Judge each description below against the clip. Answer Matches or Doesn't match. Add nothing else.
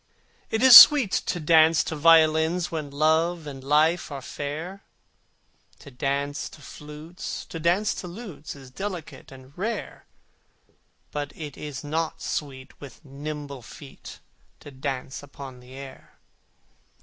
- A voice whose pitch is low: Doesn't match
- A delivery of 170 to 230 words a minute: Doesn't match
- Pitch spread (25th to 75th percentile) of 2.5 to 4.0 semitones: Matches